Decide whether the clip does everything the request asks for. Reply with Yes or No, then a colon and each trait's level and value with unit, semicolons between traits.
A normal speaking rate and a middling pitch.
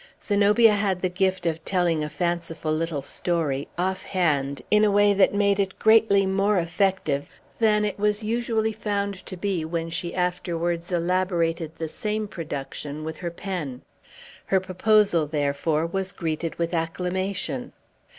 Yes: average, 150 wpm; medium, 180 Hz